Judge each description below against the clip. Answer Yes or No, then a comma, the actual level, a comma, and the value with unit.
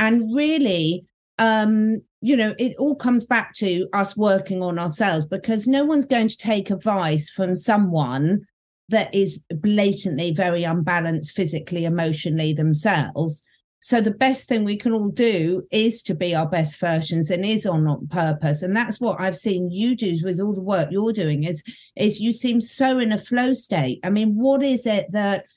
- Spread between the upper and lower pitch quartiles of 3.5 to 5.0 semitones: Yes, average, 4.7 semitones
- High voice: Yes, high, 200 Hz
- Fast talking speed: No, average, 185 wpm